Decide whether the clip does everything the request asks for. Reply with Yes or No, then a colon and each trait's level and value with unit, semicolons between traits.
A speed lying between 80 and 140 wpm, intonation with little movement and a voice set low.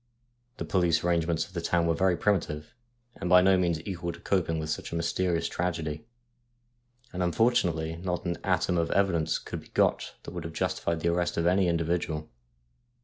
No: average, 185 wpm; narrow, 1.7 semitones; very low, 85 Hz